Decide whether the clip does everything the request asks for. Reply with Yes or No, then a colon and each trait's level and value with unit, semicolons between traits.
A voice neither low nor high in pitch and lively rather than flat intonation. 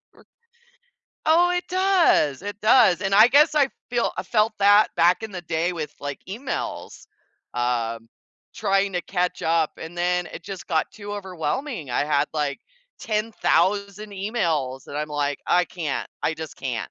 Yes: medium, 180 Hz; wide, 5.7 semitones